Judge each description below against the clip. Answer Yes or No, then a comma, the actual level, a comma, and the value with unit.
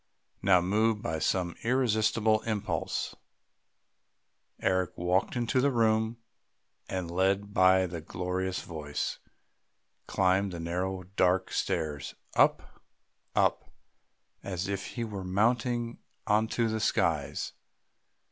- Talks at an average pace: No, slow, 105 wpm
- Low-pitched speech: Yes, very low, 95 Hz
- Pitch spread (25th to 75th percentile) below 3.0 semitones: No, average, 3.4 semitones